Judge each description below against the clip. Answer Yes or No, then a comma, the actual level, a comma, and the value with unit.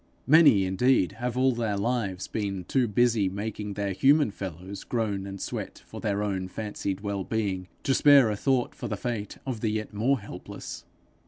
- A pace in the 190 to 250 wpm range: No, average, 180 wpm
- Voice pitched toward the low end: Yes, low, 105 Hz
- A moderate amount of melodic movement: Yes, average, 3.8 semitones